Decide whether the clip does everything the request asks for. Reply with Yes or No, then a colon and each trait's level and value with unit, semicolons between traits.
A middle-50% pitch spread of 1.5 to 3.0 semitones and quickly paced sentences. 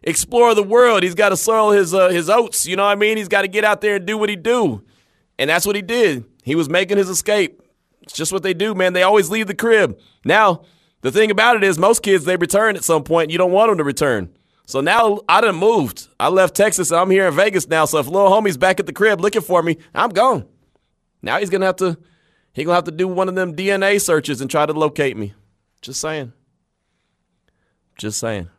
No: average, 4.3 semitones; fast, 250 wpm